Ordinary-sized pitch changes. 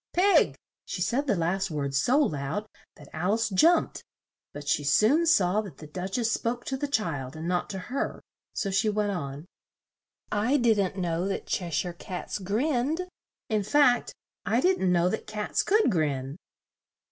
No: wide, 6.1 semitones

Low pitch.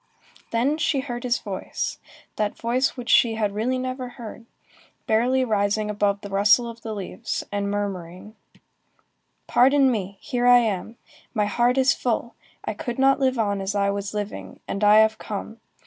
No: high, 220 Hz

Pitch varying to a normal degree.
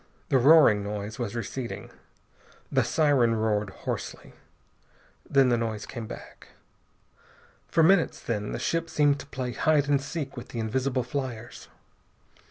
Yes: average, 4.3 semitones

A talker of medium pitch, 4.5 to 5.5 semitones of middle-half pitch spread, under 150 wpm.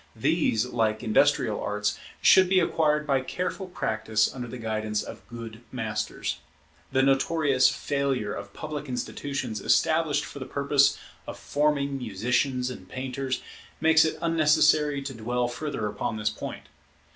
No: low, 130 Hz; average, 4.8 semitones; average, 140 wpm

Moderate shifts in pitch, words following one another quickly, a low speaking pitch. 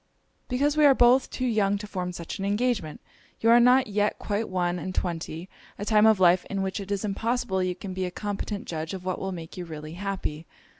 No: average, 3.5 semitones; fast, 230 wpm; high, 195 Hz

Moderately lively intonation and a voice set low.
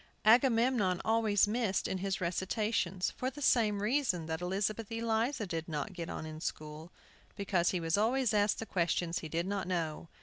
No: average, 4.7 semitones; high, 195 Hz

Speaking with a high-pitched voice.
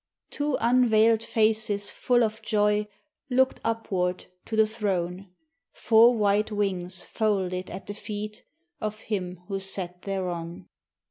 Yes: high, 210 Hz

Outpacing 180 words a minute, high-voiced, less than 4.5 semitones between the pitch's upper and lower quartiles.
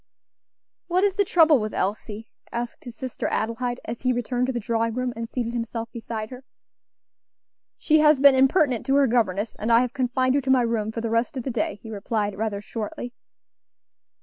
Yes: average, 200 wpm; high, 240 Hz; narrow, 2.6 semitones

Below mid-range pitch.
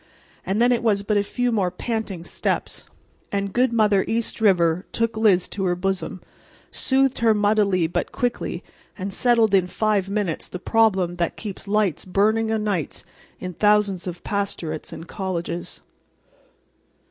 No: high, 200 Hz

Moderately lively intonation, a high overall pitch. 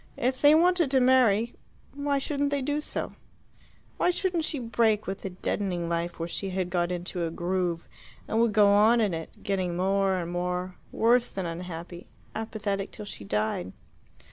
No: wide, 5.7 semitones; high, 195 Hz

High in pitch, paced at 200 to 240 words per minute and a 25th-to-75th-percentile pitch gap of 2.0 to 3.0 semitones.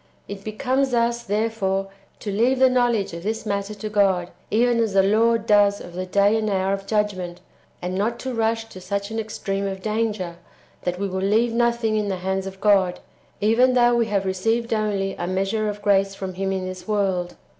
Yes: high, 205 Hz; fast, 205 wpm; average, 2.7 semitones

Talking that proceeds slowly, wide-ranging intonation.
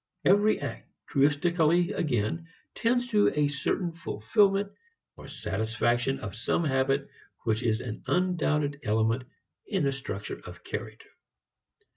Yes: slow, 120 wpm; wide, 7.1 semitones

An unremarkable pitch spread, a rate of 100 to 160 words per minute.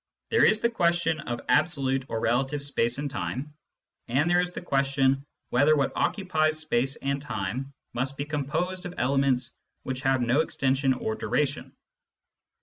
Yes: average, 3.0 semitones; average, 155 wpm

